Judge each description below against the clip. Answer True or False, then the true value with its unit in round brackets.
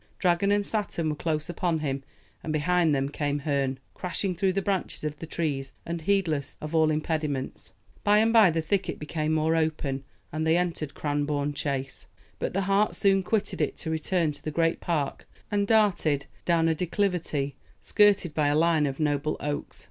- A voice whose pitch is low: False (160 Hz)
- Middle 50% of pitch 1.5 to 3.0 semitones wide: False (3.6 semitones)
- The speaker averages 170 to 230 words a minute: True (185 wpm)